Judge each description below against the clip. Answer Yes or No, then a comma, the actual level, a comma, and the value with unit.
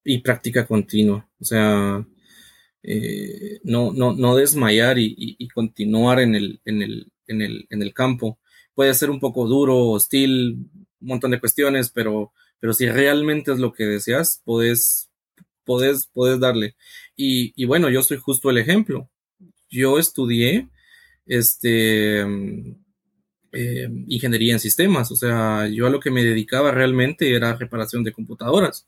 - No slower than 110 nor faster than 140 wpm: No, average, 150 wpm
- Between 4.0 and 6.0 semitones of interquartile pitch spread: No, average, 3.4 semitones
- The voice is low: Yes, low, 125 Hz